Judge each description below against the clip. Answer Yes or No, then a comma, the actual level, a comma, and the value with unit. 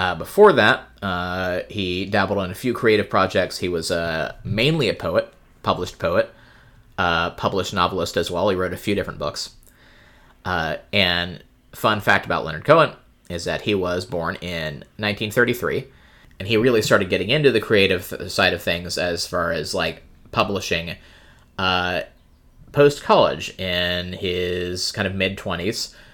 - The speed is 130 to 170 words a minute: Yes, average, 160 wpm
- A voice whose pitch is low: Yes, very low, 90 Hz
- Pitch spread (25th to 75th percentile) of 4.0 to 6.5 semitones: No, average, 2.7 semitones